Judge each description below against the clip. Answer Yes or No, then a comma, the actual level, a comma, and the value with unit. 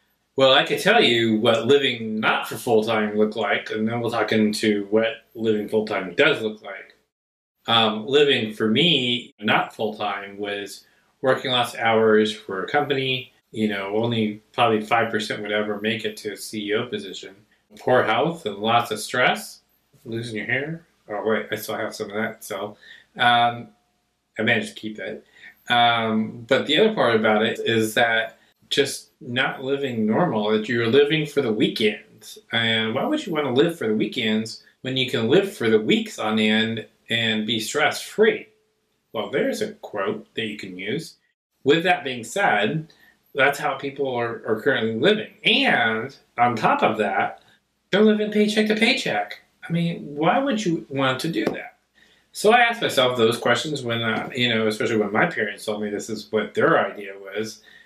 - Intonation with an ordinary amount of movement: Yes, average, 4.2 semitones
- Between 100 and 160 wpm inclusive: No, average, 185 wpm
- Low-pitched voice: Yes, low, 115 Hz